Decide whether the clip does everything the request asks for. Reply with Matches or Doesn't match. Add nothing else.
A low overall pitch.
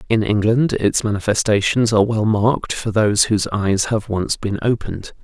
Matches